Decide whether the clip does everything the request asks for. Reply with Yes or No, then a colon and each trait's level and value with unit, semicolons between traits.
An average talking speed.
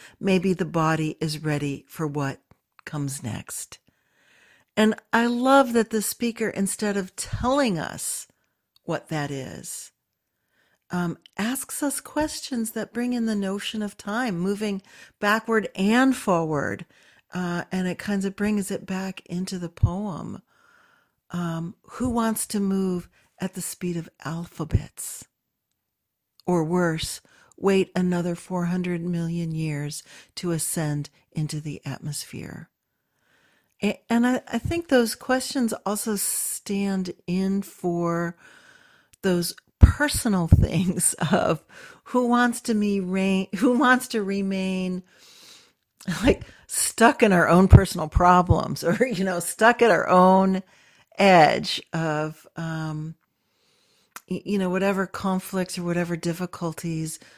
No: slow, 120 wpm